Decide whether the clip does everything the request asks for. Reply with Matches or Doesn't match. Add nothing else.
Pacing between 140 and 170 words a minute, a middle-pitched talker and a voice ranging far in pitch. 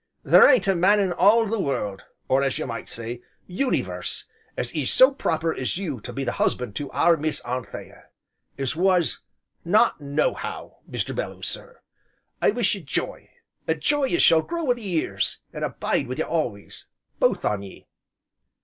Doesn't match